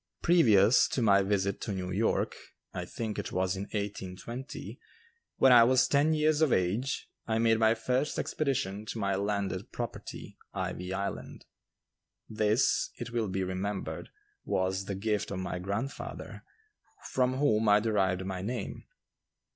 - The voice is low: Yes, low, 105 Hz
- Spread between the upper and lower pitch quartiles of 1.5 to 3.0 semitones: No, average, 3.9 semitones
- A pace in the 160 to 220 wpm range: No, average, 145 wpm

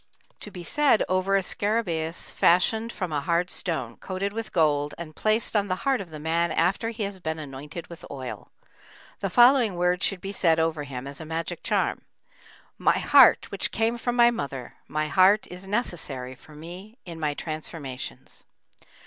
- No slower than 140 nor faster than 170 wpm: No, average, 180 wpm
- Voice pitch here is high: No, medium, 175 Hz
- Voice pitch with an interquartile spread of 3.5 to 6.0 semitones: Yes, average, 4.7 semitones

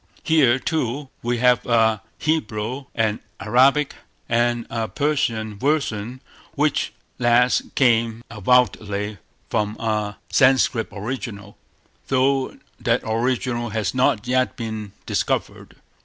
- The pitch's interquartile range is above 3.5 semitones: No, average, 2.9 semitones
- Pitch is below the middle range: Yes, low, 120 Hz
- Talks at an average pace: No, slow, 105 wpm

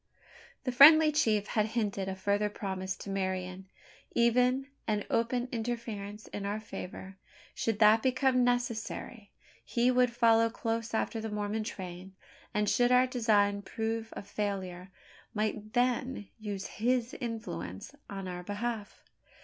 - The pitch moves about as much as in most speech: Yes, average, 3.0 semitones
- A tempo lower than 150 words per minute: Yes, slow, 135 wpm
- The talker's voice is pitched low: No, high, 220 Hz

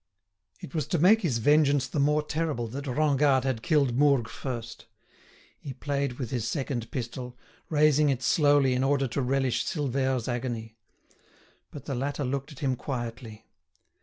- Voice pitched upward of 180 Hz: No, low, 135 Hz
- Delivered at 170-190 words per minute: No, average, 160 wpm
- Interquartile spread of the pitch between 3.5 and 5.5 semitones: No, average, 2.9 semitones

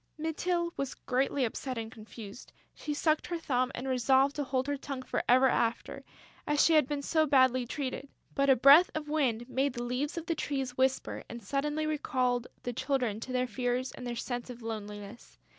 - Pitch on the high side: Yes, very high, 260 Hz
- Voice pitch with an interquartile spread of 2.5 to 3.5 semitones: Yes, average, 2.9 semitones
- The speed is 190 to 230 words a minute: Yes, average, 195 wpm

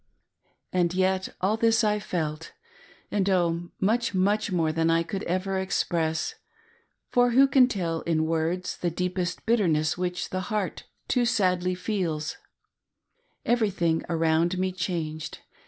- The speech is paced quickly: No, slow, 135 wpm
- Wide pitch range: No, average, 3.5 semitones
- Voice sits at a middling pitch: Yes, medium, 180 Hz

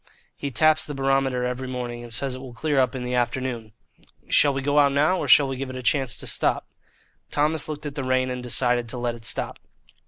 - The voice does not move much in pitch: Yes, narrow, 2.3 semitones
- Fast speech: Yes, fast, 240 wpm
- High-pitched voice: No, low, 130 Hz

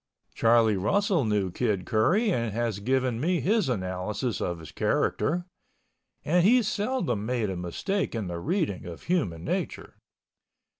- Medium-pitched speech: No, low, 120 Hz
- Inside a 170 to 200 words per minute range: No, average, 145 wpm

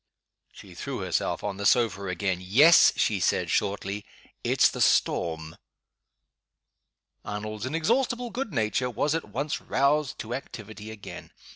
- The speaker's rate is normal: No, slow, 130 wpm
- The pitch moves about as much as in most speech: No, wide, 6.8 semitones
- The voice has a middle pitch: No, low, 110 Hz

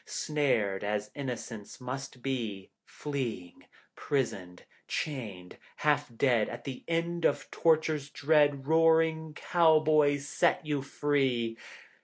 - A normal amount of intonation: Yes, average, 4.9 semitones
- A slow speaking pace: Yes, slow, 105 wpm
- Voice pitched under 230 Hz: Yes, medium, 140 Hz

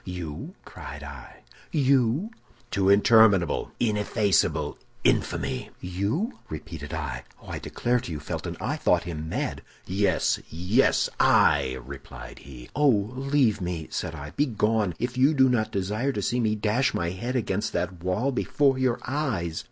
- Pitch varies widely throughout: Yes, wide, 6.9 semitones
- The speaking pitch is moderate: No, low, 105 Hz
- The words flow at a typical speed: Yes, average, 150 wpm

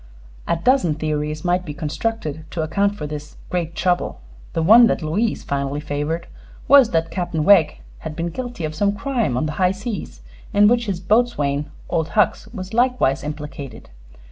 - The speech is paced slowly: No, average, 170 wpm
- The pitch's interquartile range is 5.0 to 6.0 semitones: Yes, wide, 5.4 semitones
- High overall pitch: No, medium, 170 Hz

